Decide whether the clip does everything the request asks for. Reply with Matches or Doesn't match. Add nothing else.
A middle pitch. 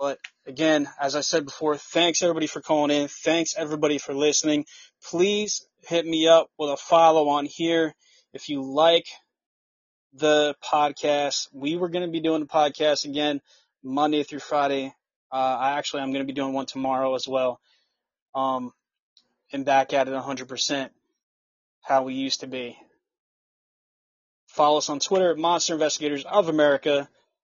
Matches